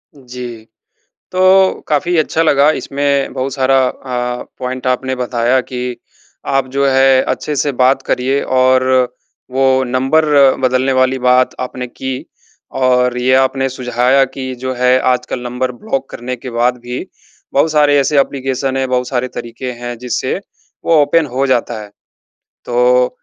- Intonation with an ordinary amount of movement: No, narrow, 1.4 semitones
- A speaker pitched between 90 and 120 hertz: No, low, 130 Hz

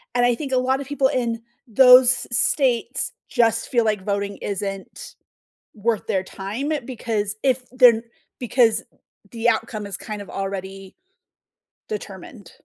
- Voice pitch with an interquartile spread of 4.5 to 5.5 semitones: No, average, 3.8 semitones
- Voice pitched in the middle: No, high, 230 Hz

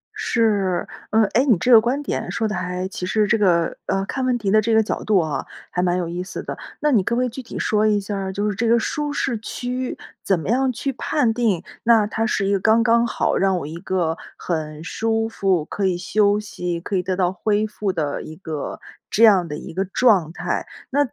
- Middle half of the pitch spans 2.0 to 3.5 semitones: No, average, 4.0 semitones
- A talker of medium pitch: No, high, 205 Hz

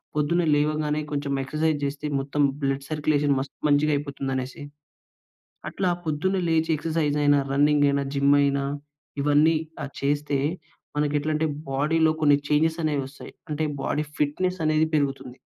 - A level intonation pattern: Yes, narrow, 1.7 semitones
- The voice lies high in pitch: No, medium, 150 Hz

